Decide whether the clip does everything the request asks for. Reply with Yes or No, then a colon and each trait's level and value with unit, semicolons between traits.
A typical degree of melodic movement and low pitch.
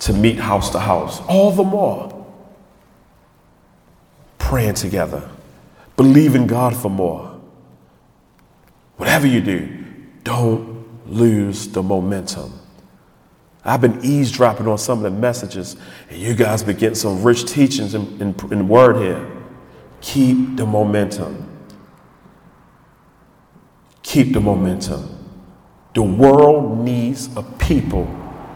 Yes: average, 4.3 semitones; low, 115 Hz